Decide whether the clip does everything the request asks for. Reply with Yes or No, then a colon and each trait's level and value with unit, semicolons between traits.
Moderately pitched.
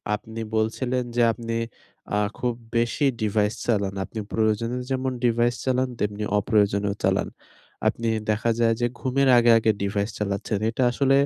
No: low, 115 Hz